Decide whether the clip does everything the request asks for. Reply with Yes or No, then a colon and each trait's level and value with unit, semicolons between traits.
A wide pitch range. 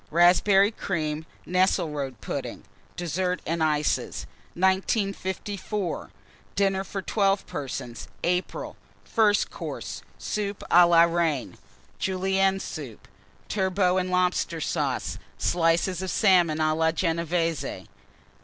No: average, 2.9 semitones